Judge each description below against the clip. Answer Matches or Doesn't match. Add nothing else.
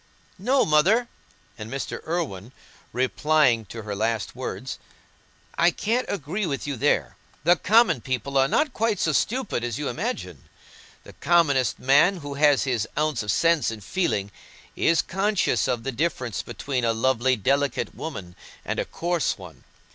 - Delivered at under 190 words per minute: Matches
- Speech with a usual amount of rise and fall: Doesn't match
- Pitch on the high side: Doesn't match